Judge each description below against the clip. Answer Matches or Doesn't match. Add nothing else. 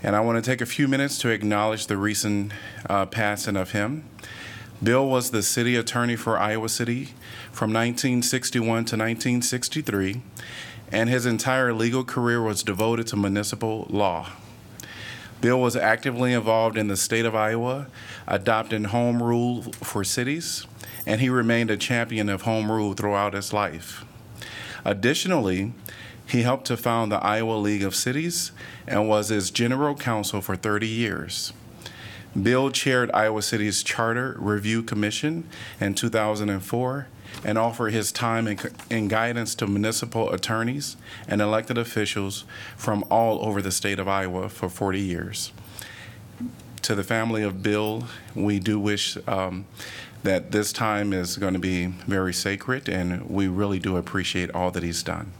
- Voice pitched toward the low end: Matches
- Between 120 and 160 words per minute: Matches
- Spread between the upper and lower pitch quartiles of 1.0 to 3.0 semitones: Matches